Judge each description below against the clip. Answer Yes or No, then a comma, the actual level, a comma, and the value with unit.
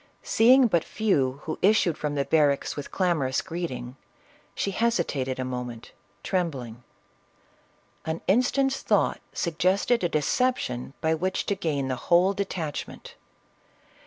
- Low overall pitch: No, medium, 165 Hz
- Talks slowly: Yes, slow, 130 wpm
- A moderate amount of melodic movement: No, wide, 6.2 semitones